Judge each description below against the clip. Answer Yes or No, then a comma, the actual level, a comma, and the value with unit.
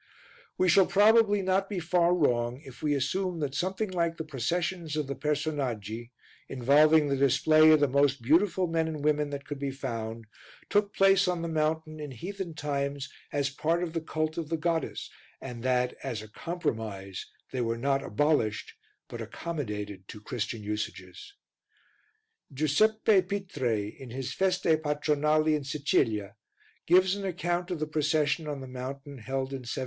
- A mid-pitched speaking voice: Yes, medium, 150 Hz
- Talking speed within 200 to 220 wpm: No, average, 165 wpm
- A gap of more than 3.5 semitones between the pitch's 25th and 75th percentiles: Yes, average, 4.5 semitones